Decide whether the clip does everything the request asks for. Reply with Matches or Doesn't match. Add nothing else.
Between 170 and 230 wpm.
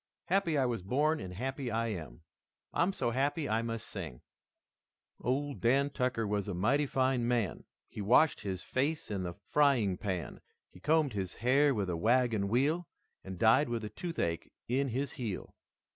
Matches